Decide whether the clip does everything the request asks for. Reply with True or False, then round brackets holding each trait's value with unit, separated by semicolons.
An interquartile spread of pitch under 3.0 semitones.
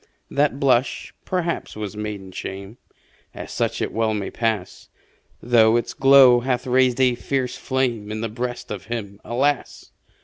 False (3.5 semitones)